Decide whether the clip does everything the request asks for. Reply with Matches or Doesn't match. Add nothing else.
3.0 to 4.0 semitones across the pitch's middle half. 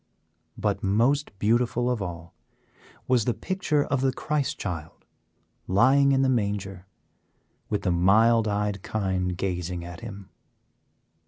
Doesn't match